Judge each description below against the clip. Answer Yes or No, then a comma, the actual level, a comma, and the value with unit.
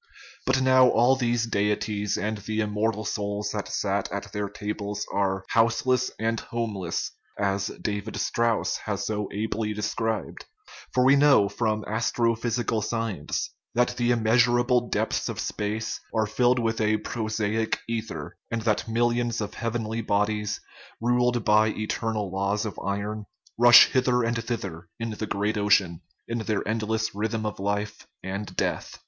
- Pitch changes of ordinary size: No, narrow, 2.1 semitones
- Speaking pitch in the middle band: No, low, 110 Hz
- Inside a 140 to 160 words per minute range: Yes, average, 150 wpm